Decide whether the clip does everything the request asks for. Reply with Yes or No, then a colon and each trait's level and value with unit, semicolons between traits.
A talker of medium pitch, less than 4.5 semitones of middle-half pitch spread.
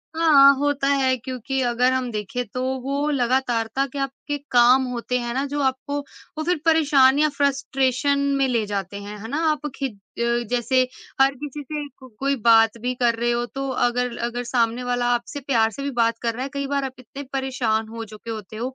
No: very high, 255 Hz; average, 2.8 semitones